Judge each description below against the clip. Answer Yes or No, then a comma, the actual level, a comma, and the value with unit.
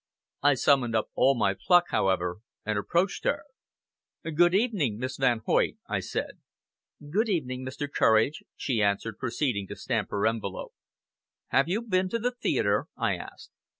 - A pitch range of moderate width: No, wide, 7.9 semitones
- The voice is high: No, low, 130 Hz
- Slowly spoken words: No, average, 155 wpm